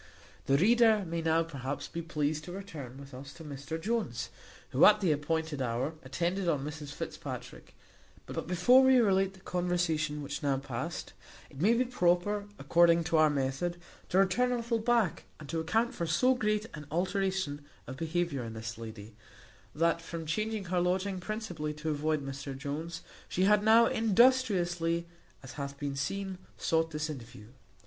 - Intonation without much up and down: No, average, 5.1 semitones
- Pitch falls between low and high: Yes, medium, 165 Hz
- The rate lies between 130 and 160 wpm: No, average, 170 wpm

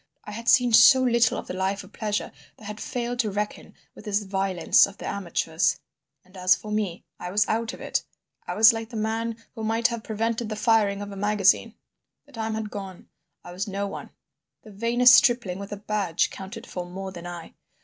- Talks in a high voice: Yes, high, 210 Hz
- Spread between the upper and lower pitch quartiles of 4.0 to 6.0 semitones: No, average, 2.7 semitones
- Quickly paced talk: Yes, fast, 215 wpm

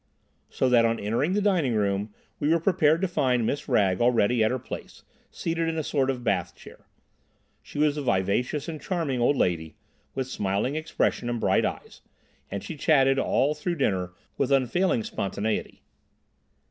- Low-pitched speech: Yes, low, 130 Hz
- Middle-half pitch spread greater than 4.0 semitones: Yes, wide, 5.6 semitones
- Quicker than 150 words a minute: Yes, average, 170 wpm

